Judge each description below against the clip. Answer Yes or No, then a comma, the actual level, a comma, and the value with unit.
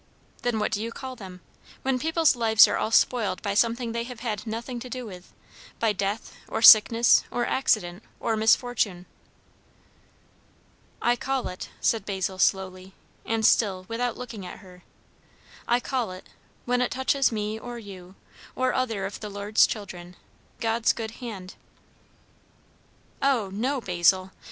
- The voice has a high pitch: Yes, high, 225 Hz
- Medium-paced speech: Yes, average, 150 wpm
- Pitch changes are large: No, average, 3.9 semitones